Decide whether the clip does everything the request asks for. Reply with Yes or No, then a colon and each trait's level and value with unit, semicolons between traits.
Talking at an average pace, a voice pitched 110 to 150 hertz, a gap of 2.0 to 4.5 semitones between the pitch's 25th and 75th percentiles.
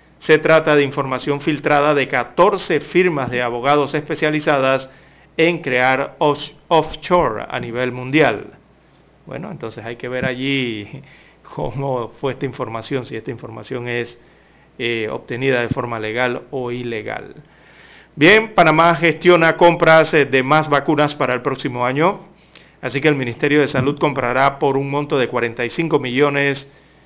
Yes: average, 140 wpm; medium, 140 Hz; average, 3.5 semitones